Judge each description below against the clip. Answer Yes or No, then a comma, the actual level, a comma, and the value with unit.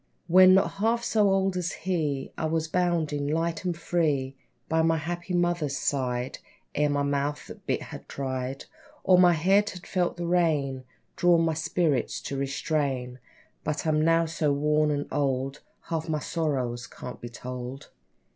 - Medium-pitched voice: Yes, medium, 155 Hz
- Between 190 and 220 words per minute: No, average, 165 wpm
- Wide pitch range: No, average, 3.9 semitones